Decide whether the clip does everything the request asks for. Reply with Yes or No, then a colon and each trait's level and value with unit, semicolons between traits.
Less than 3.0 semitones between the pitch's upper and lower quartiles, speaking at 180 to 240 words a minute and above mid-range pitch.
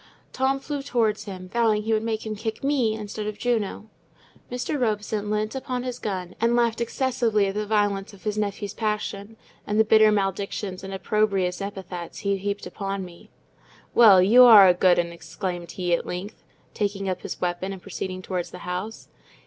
Yes: narrow, 2.5 semitones; average, 185 wpm; high, 210 Hz